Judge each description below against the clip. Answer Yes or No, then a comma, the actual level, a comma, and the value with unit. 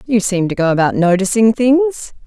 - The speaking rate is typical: Yes, average, 185 wpm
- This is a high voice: Yes, high, 220 Hz